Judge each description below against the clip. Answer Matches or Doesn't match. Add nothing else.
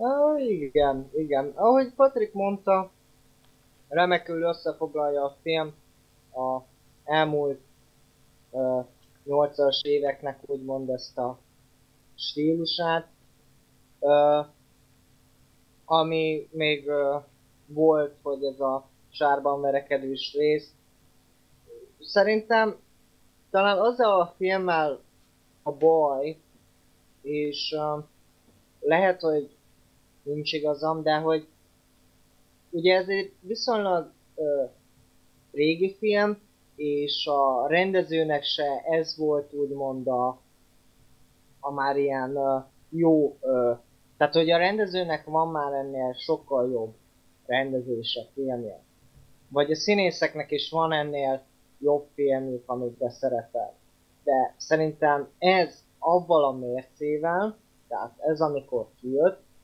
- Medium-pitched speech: Matches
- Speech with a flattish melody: Doesn't match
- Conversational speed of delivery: Doesn't match